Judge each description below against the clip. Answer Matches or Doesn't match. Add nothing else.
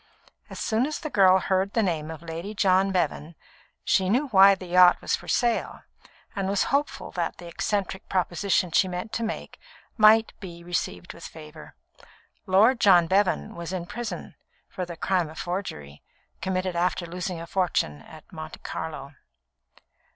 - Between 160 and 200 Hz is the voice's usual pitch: Matches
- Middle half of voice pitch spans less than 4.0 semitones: Matches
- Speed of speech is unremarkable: Matches